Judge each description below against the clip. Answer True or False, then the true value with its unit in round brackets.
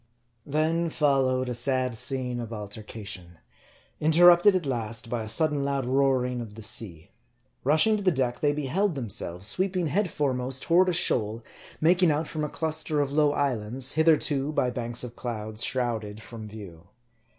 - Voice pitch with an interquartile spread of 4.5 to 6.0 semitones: True (5.3 semitones)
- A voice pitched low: True (130 Hz)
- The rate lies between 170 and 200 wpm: False (160 wpm)